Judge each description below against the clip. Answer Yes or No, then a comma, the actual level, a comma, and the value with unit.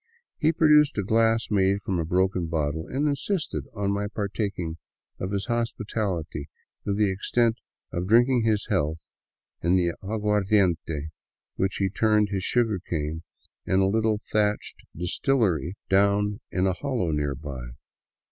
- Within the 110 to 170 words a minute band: Yes, average, 145 wpm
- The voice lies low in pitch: Yes, low, 100 Hz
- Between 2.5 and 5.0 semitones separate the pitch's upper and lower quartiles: Yes, average, 3.9 semitones